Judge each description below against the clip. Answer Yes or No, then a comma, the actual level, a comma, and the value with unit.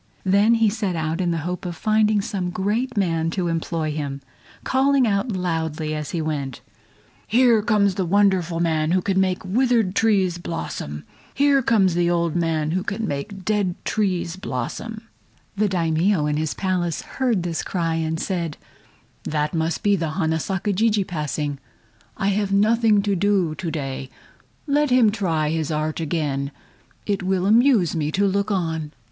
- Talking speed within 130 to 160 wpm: No, average, 170 wpm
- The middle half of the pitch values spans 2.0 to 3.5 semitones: No, average, 4.3 semitones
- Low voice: No, medium, 180 Hz